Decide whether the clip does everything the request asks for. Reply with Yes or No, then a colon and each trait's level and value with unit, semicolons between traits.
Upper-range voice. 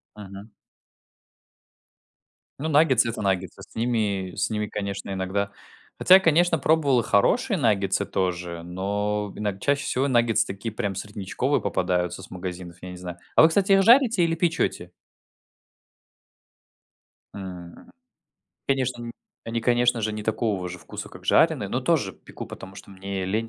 No: low, 105 Hz